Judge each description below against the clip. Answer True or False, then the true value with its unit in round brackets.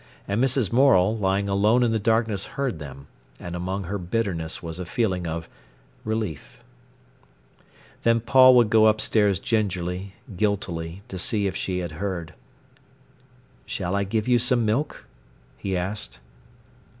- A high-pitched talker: False (100 Hz)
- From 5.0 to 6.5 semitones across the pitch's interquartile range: False (3.9 semitones)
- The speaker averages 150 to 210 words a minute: False (140 wpm)